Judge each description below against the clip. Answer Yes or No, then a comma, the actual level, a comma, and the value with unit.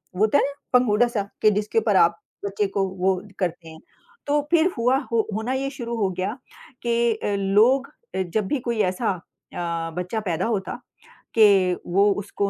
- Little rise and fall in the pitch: No, average, 3.9 semitones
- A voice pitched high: Yes, high, 210 Hz